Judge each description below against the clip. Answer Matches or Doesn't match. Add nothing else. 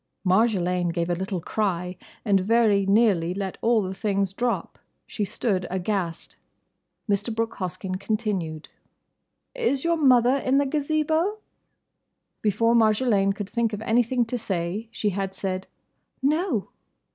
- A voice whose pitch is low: Doesn't match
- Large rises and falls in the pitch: Doesn't match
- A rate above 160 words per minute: Doesn't match